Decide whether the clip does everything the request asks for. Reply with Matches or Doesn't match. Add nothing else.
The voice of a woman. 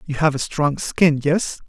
Doesn't match